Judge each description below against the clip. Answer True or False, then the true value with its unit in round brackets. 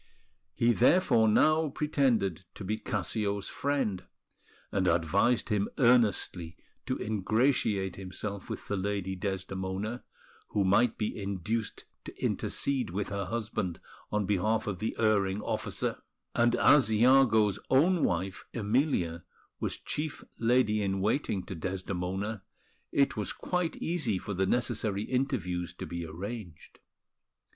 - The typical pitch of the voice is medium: False (105 Hz)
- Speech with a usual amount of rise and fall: True (4.0 semitones)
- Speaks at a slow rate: True (125 wpm)